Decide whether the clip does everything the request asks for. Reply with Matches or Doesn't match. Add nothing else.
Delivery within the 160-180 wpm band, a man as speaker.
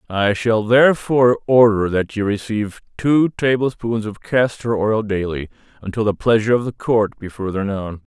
Matches